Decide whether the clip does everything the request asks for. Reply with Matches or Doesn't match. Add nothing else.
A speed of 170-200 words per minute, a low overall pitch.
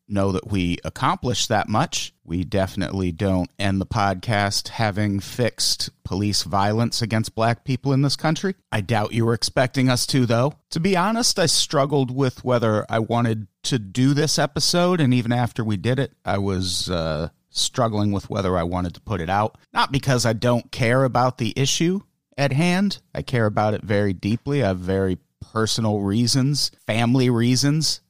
Matches